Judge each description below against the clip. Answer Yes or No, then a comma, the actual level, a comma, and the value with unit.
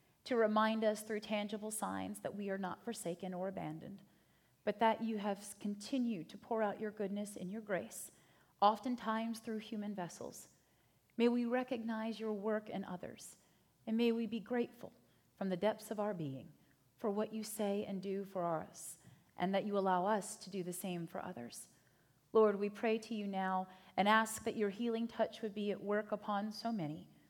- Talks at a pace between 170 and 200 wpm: Yes, average, 190 wpm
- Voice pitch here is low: No, high, 210 Hz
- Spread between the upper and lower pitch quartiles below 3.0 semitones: Yes, narrow, 2.4 semitones